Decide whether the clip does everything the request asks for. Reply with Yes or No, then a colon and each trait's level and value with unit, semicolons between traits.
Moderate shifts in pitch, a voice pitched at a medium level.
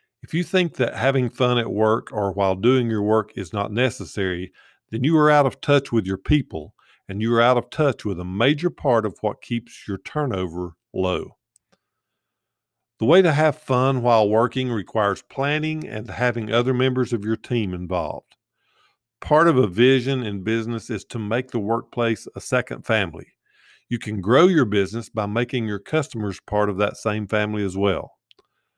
No: average, 3.7 semitones; low, 115 Hz